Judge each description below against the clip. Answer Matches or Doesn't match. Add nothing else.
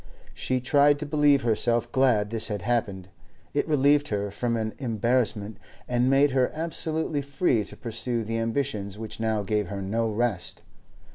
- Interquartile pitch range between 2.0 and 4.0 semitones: Doesn't match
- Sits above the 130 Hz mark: Doesn't match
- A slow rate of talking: Doesn't match